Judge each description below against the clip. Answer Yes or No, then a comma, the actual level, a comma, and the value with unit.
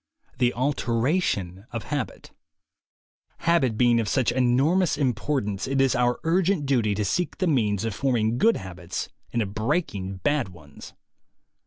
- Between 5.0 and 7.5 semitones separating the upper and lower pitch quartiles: Yes, wide, 5.6 semitones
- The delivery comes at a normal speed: Yes, average, 150 wpm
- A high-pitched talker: No, low, 120 Hz